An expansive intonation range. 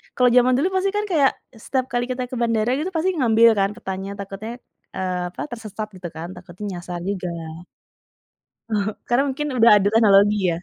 No: average, 4.8 semitones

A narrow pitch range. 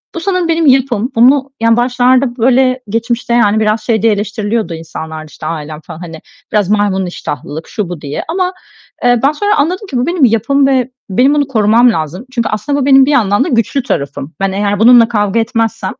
No: average, 4.6 semitones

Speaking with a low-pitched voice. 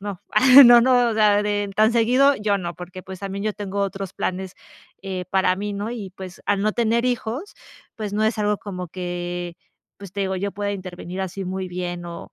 No: high, 200 Hz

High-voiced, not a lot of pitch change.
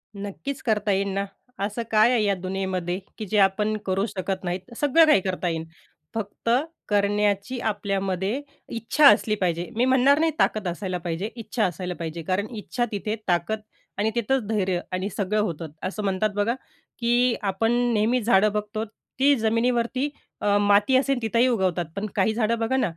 No: high, 210 Hz; average, 3.4 semitones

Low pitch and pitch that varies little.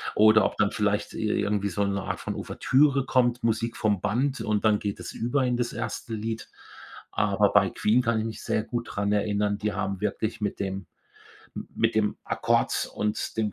Yes: low, 110 Hz; narrow, 2.2 semitones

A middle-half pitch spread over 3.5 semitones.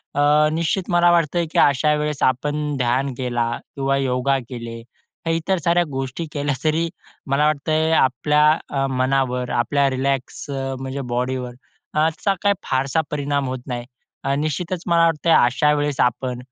No: average, 2.9 semitones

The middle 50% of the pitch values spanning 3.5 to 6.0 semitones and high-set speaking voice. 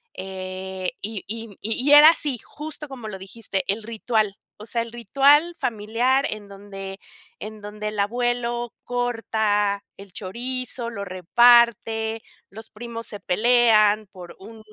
No: average, 3.1 semitones; high, 220 Hz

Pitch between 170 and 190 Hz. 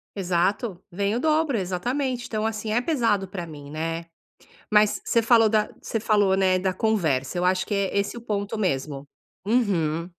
No: high, 200 Hz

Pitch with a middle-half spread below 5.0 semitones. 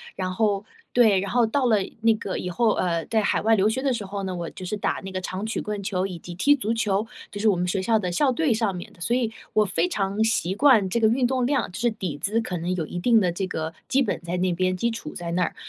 Yes: average, 3.9 semitones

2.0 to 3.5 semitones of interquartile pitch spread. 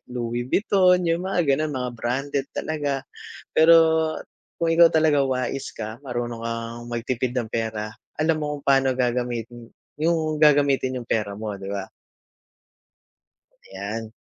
No: average, 4.7 semitones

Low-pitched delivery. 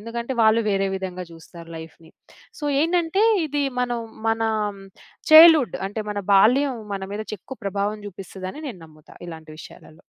No: high, 210 Hz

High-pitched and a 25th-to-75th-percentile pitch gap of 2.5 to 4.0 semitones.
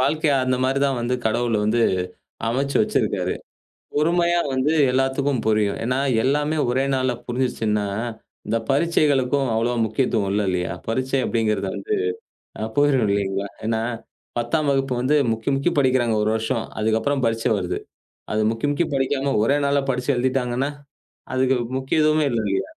No: low, 130 Hz; average, 3.7 semitones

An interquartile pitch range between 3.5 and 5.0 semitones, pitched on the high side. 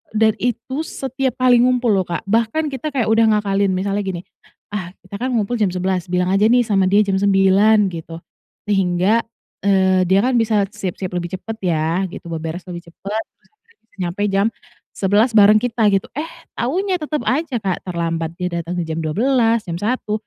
Yes: average, 4.2 semitones; high, 200 Hz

